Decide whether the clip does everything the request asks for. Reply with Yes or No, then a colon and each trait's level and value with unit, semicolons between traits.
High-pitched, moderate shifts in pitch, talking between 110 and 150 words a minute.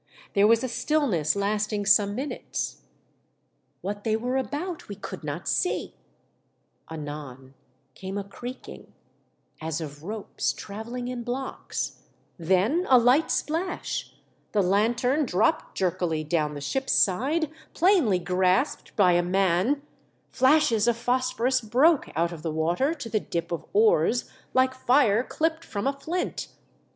No: high, 220 Hz; wide, 6.6 semitones; average, 140 wpm